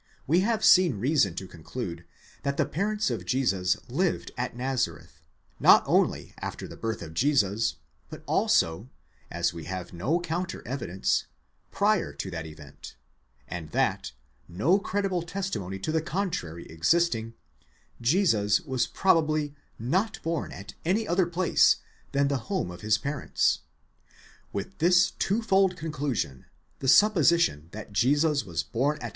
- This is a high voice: No, low, 135 Hz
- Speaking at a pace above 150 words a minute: No, average, 140 wpm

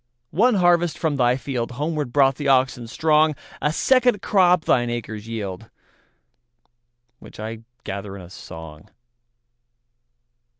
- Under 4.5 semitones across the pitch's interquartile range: No, wide, 5.6 semitones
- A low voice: Yes, low, 125 Hz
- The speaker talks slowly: Yes, slow, 110 wpm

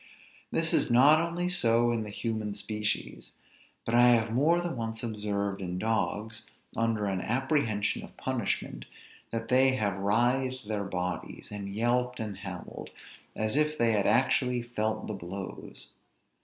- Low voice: Yes, low, 110 Hz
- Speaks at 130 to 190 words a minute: Yes, average, 150 wpm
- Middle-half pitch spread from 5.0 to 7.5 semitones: No, average, 3.3 semitones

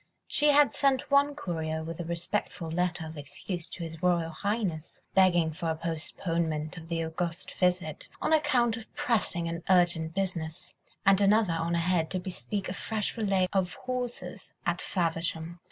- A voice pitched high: No, medium, 175 Hz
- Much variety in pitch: No, average, 3.5 semitones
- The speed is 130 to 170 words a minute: Yes, average, 165 wpm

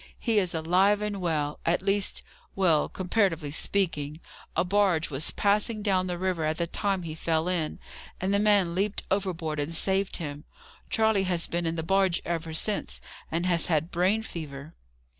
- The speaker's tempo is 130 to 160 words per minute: No, average, 175 wpm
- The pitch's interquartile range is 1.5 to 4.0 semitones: Yes, average, 3.5 semitones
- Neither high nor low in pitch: Yes, medium, 180 Hz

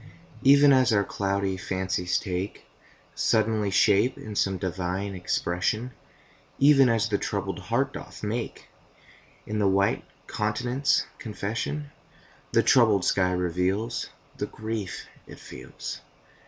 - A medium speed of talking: No, slow, 115 wpm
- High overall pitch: No, low, 105 Hz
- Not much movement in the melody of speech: No, average, 3.5 semitones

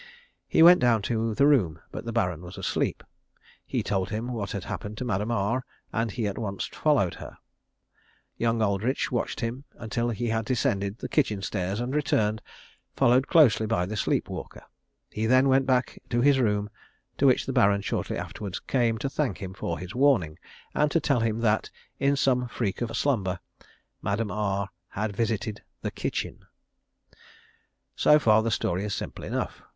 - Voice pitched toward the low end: Yes, low, 115 Hz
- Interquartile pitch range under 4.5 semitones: Yes, average, 3.9 semitones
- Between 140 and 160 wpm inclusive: No, average, 175 wpm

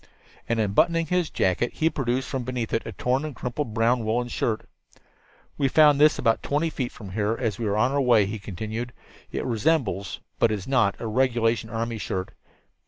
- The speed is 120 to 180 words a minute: No, average, 195 wpm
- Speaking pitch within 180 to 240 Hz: No, low, 120 Hz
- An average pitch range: Yes, average, 3.5 semitones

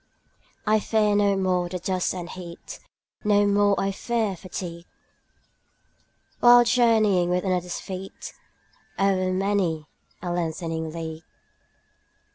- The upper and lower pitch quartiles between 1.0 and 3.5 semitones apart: Yes, average, 2.7 semitones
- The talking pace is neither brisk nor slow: No, slow, 115 wpm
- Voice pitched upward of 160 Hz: Yes, medium, 185 Hz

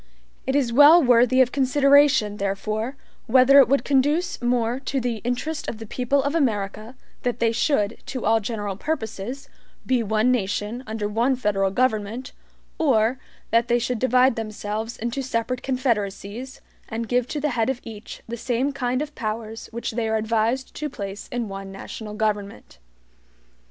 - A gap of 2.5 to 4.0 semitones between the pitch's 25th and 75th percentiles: Yes, average, 3.3 semitones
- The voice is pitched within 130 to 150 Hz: No, high, 235 Hz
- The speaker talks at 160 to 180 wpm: Yes, average, 165 wpm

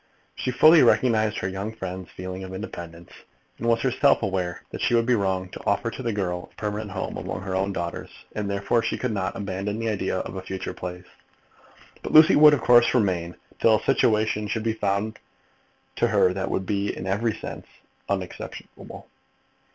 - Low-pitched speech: Yes, low, 100 Hz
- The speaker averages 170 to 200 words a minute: Yes, average, 195 wpm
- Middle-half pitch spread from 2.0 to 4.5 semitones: Yes, average, 3.5 semitones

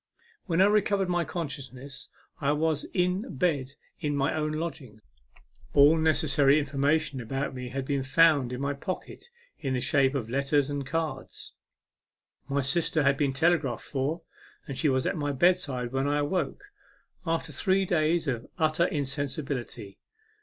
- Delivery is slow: No, average, 155 wpm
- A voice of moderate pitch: Yes, medium, 145 Hz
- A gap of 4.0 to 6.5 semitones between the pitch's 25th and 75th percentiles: No, average, 3.2 semitones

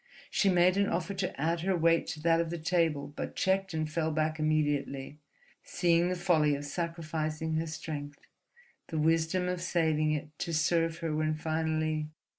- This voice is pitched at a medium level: Yes, medium, 160 Hz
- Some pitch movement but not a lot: No, narrow, 1.9 semitones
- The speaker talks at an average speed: Yes, average, 175 wpm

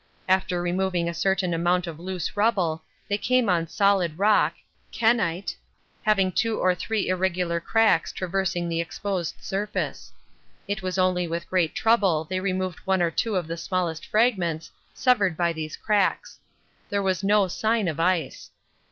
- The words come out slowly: No, average, 155 wpm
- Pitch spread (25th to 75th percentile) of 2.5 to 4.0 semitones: Yes, average, 2.9 semitones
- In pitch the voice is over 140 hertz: Yes, medium, 185 Hz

